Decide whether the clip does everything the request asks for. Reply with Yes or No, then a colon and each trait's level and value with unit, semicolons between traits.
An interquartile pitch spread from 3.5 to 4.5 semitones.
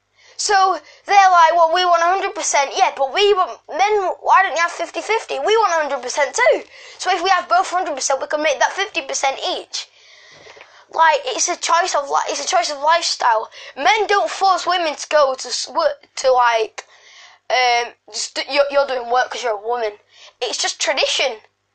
No: average, 5.2 semitones